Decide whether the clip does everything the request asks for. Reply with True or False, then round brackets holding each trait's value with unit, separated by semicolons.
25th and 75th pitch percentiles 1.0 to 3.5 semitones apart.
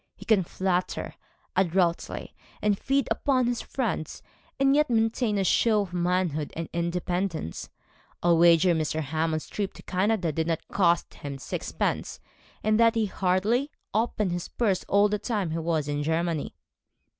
False (4.5 semitones)